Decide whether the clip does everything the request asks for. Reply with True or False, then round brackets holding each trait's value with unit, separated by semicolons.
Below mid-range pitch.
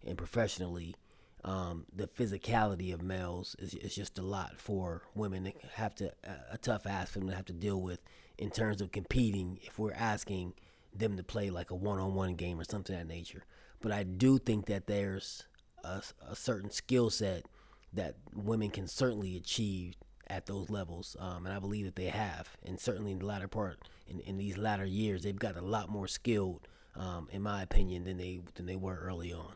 True (95 Hz)